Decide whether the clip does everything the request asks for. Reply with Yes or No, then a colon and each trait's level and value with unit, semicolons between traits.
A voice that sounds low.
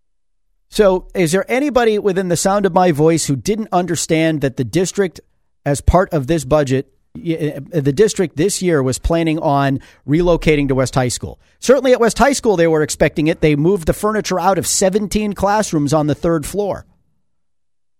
No: medium, 165 Hz